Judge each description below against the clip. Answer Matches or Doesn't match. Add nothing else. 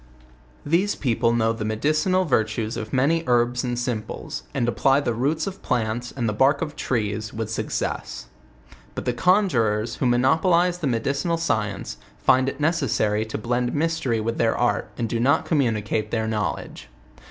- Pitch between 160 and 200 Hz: Doesn't match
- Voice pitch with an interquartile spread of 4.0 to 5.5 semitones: Matches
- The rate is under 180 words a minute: Matches